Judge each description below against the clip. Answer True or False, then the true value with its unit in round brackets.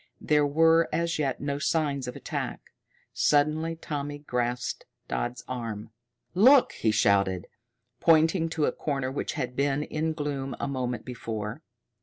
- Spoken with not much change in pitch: False (4.1 semitones)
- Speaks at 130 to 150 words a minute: True (140 wpm)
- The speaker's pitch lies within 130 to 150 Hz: True (140 Hz)